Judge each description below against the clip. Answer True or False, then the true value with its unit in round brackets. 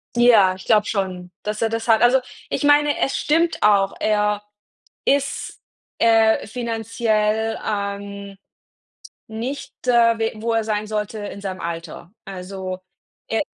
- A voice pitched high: True (215 Hz)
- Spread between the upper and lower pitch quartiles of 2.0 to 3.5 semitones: True (2.5 semitones)